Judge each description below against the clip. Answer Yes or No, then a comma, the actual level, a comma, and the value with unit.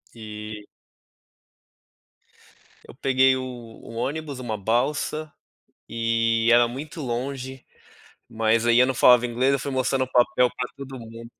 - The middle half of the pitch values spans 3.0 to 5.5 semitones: No, narrow, 2.4 semitones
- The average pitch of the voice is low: Yes, low, 125 Hz